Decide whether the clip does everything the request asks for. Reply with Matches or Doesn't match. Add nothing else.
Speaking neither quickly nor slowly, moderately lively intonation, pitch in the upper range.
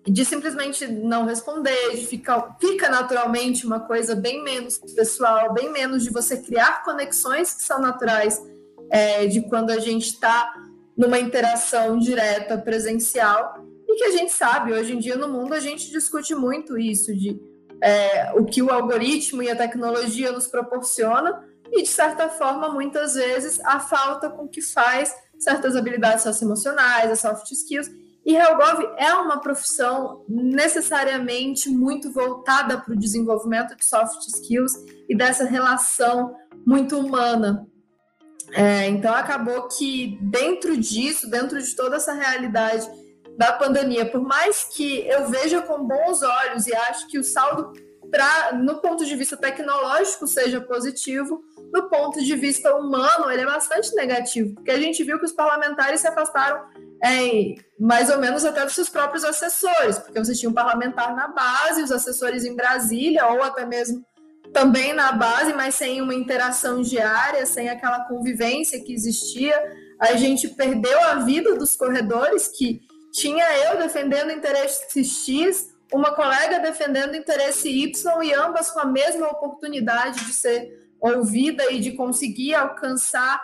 Matches